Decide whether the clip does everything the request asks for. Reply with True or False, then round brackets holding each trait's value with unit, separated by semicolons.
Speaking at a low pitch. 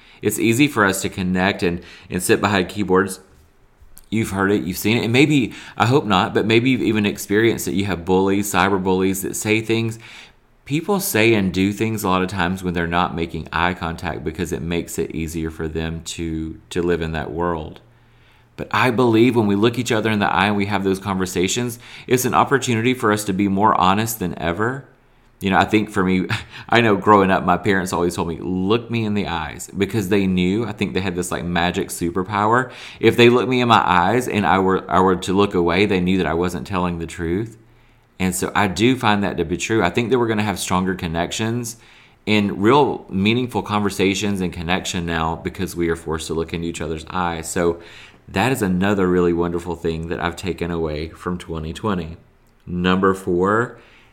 True (95 Hz)